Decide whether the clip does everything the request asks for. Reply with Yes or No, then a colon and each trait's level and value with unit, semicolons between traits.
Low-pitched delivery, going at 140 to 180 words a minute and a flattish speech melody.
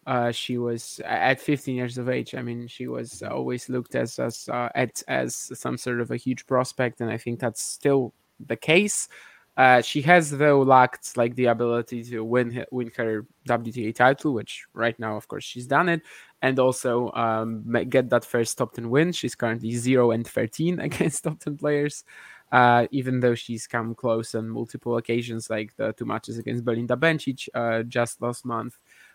No: low, 120 Hz; average, 190 wpm; narrow, 2.1 semitones